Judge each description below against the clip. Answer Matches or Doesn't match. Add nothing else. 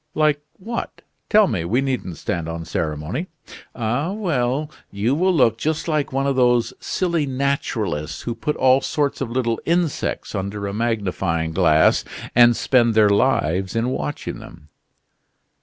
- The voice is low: Matches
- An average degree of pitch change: Doesn't match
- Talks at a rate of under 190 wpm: Matches